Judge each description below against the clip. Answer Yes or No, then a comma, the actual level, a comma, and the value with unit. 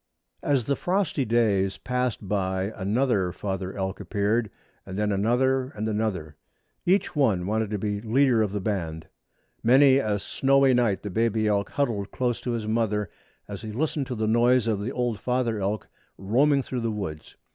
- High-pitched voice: No, low, 110 Hz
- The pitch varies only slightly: No, average, 3.9 semitones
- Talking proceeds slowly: No, average, 175 wpm